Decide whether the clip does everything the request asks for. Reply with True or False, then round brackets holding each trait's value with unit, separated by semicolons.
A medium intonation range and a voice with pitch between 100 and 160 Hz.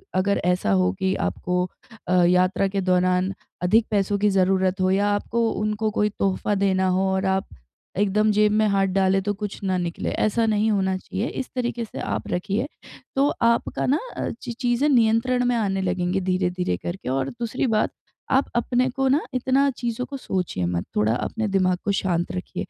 False (3.6 semitones; 195 Hz)